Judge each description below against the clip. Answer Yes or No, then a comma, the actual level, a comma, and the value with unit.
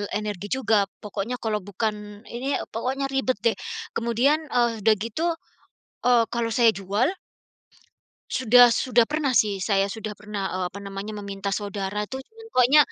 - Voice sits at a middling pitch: No, high, 220 Hz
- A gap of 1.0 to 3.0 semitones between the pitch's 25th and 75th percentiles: No, average, 3.4 semitones